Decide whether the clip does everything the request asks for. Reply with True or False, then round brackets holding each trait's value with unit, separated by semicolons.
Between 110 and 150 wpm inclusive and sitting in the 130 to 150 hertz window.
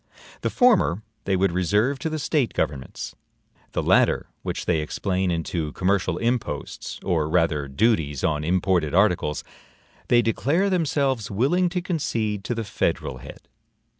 False (140 wpm; 100 Hz)